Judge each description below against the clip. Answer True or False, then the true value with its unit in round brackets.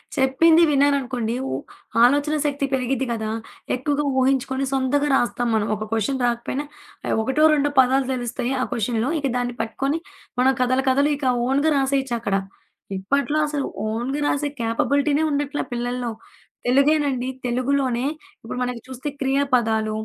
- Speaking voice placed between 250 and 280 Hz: True (265 Hz)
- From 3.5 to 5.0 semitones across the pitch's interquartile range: False (2.6 semitones)